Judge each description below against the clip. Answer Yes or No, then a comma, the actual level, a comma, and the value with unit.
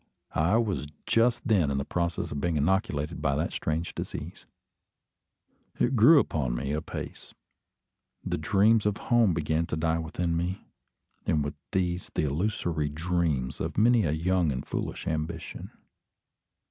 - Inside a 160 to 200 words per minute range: No, average, 145 wpm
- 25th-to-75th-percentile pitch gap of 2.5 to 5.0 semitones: Yes, average, 4.2 semitones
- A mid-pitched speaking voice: No, very low, 85 Hz